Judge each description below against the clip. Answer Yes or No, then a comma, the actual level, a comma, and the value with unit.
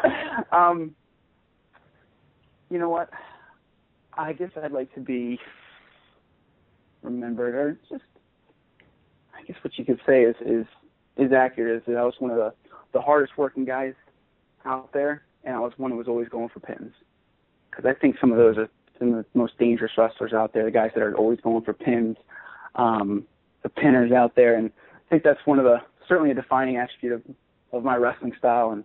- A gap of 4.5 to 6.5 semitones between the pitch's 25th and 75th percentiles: No, average, 3.3 semitones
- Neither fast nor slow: Yes, average, 190 wpm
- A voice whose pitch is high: No, low, 125 Hz